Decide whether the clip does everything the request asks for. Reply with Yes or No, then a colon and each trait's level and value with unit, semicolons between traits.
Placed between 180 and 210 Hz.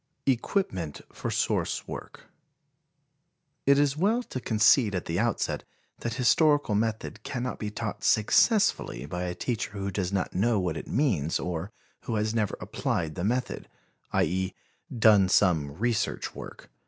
No: low, 105 Hz